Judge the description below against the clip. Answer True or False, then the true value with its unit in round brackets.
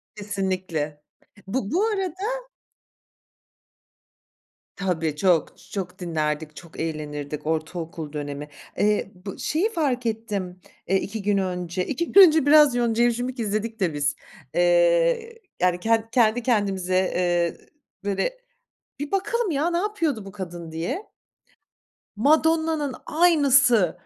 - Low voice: False (210 Hz)